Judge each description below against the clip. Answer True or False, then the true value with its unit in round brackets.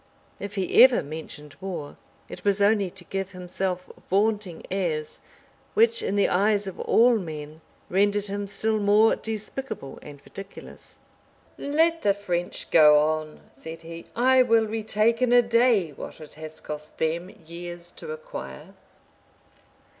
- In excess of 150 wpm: False (145 wpm)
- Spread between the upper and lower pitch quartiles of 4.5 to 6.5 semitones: True (5.1 semitones)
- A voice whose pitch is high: True (195 Hz)